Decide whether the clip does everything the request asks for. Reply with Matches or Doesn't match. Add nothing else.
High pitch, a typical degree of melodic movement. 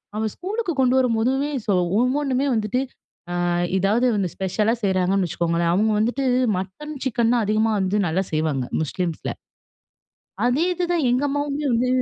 Doesn't match